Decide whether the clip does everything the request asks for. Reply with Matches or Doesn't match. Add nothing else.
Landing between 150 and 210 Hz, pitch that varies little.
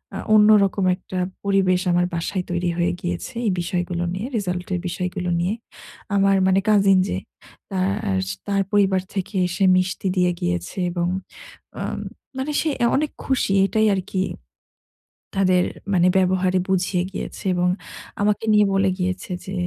Matches